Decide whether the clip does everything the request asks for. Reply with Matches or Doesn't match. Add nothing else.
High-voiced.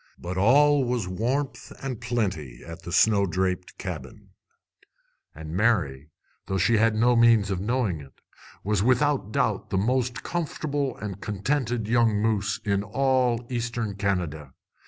Doesn't match